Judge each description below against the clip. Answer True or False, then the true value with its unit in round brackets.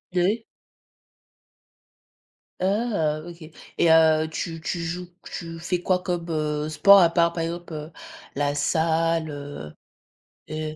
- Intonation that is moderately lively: False (2.0 semitones)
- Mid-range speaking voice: True (165 Hz)